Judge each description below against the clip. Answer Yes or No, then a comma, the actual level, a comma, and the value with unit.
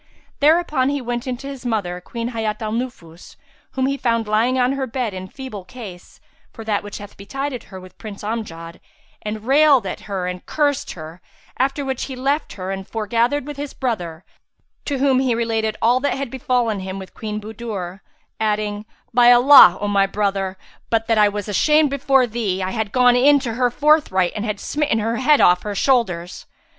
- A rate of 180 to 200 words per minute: Yes, average, 195 wpm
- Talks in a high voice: Yes, high, 225 Hz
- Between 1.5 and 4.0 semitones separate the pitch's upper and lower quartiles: No, average, 4.6 semitones